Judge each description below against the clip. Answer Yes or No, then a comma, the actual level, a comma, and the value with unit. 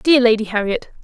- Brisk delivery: No, average, 175 wpm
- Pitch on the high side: Yes, high, 240 Hz